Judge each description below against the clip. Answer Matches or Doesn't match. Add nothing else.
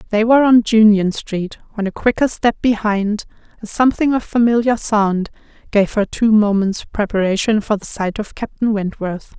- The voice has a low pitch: Doesn't match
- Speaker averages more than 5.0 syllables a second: Doesn't match